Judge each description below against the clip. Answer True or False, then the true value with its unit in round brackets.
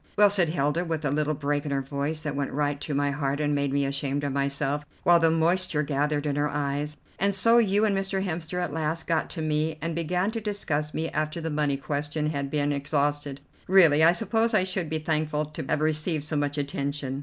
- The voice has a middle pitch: True (150 Hz)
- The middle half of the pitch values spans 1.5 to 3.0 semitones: True (2.6 semitones)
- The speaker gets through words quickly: True (230 wpm)